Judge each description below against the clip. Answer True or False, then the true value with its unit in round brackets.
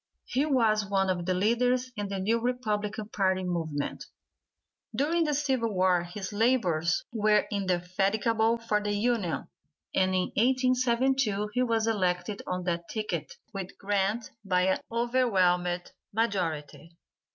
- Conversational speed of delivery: False (130 wpm)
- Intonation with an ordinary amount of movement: True (4.2 semitones)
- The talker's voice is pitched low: False (205 Hz)